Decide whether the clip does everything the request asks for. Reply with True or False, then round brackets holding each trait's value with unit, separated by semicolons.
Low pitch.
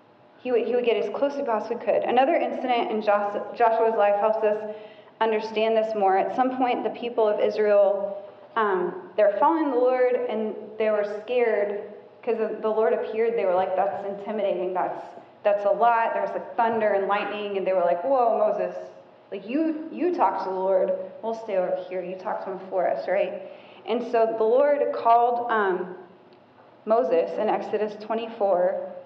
False (215 Hz)